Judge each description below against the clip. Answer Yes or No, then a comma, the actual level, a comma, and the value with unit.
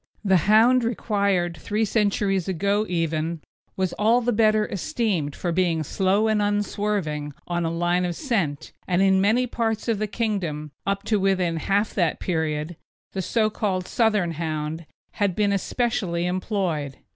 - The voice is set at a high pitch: Yes, high, 195 Hz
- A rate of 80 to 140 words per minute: No, average, 155 wpm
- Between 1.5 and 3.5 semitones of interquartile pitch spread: No, average, 4.0 semitones